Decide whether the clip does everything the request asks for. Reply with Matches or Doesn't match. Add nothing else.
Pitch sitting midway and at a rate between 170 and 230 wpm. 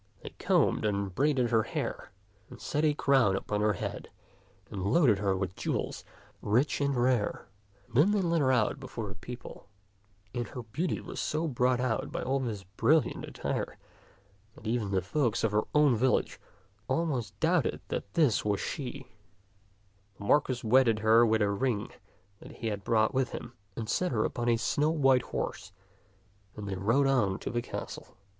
Doesn't match